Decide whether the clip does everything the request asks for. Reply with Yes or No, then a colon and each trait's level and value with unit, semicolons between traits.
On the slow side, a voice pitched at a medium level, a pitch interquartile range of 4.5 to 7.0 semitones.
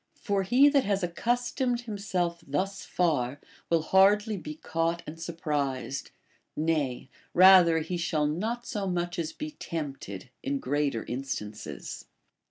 Yes: slow, 130 wpm; medium, 170 Hz; average, 5.2 semitones